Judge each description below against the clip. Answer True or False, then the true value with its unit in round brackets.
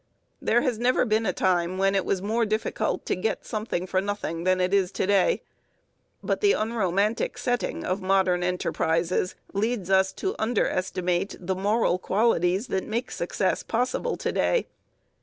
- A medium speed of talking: True (160 wpm)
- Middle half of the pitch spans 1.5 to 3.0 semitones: False (3.5 semitones)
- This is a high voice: True (195 Hz)